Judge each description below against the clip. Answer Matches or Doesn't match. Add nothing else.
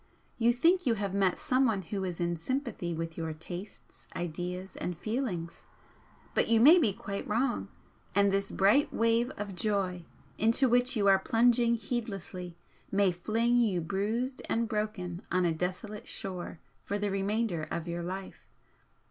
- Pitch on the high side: Matches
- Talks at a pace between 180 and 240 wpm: Doesn't match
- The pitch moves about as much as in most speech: Matches